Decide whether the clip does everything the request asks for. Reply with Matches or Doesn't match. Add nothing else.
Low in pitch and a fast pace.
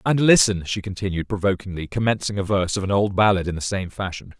Matches